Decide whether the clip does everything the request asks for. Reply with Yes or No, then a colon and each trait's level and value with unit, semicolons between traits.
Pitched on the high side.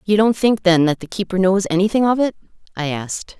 Yes: high, 195 Hz